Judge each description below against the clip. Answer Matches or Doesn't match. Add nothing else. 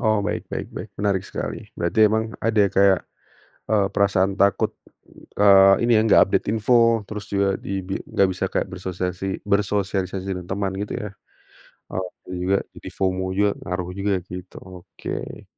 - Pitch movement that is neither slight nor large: Doesn't match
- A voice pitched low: Matches